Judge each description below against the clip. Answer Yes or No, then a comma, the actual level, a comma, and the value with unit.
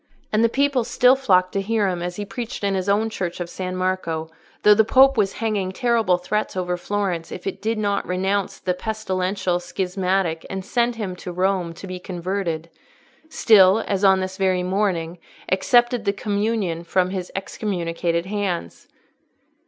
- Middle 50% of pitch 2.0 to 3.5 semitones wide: Yes, average, 2.7 semitones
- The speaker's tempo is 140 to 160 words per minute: No, average, 170 wpm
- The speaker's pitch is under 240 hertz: Yes, high, 190 Hz